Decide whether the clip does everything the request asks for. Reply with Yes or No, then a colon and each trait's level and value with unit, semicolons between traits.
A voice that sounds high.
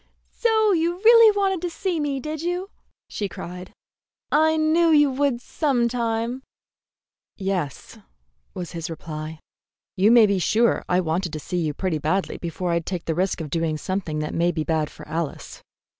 Yes: high, 195 Hz